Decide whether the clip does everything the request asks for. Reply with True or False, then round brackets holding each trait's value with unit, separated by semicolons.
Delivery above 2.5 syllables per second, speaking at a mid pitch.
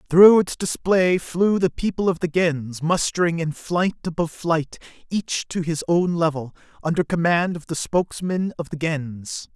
True (4.5 syllables/s; 170 Hz)